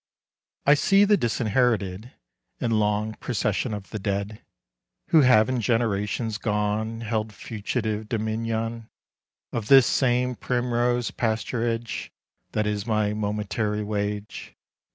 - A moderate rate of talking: No, slow, 110 wpm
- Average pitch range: No, narrow, 2.3 semitones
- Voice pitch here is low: Yes, low, 110 Hz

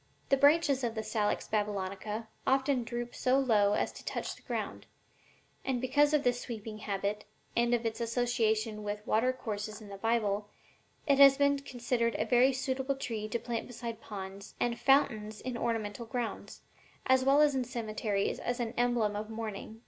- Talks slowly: No, average, 170 wpm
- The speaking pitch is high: Yes, high, 235 Hz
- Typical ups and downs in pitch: Yes, average, 3.3 semitones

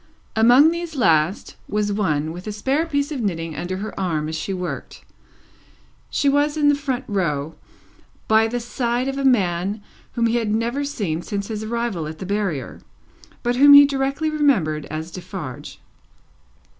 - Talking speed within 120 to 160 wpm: No, average, 170 wpm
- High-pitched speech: Yes, high, 215 Hz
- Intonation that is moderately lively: No, wide, 7.6 semitones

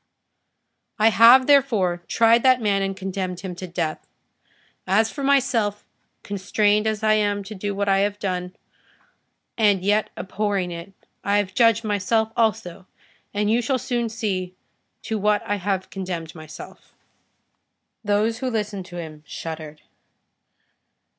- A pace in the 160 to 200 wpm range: No, average, 140 wpm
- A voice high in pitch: Yes, high, 205 Hz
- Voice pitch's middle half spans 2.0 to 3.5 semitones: Yes, average, 3.0 semitones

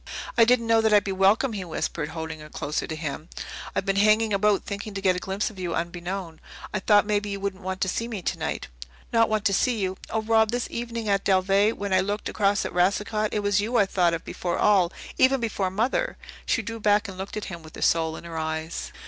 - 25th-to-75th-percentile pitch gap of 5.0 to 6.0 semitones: No, average, 2.9 semitones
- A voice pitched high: Yes, high, 200 Hz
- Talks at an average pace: No, fast, 240 wpm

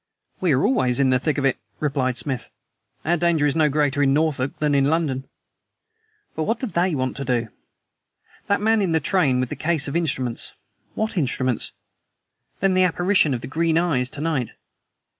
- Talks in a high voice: No, medium, 150 Hz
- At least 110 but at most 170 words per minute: No, average, 190 wpm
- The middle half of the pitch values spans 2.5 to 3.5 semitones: No, average, 4.5 semitones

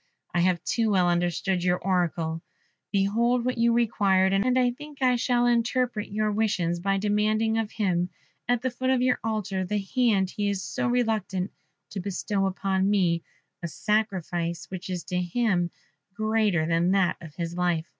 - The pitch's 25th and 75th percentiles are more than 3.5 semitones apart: Yes, average, 4.0 semitones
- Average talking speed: Yes, average, 170 wpm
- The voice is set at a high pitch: Yes, high, 200 Hz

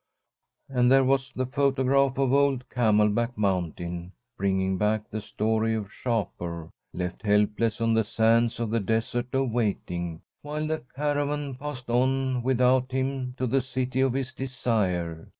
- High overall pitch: No, low, 120 Hz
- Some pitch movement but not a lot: Yes, average, 4.0 semitones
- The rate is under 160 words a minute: Yes, average, 150 wpm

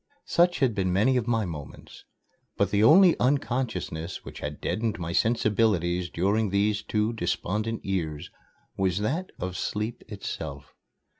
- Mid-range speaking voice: No, low, 105 Hz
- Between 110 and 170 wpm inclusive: Yes, average, 140 wpm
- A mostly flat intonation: No, average, 4.2 semitones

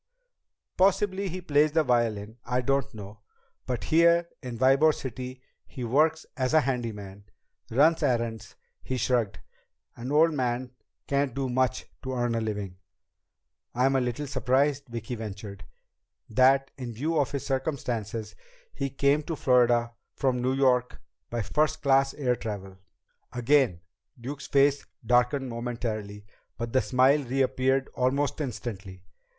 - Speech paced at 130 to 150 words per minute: Yes, slow, 135 wpm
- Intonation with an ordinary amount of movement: Yes, average, 3.1 semitones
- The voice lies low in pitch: Yes, low, 130 Hz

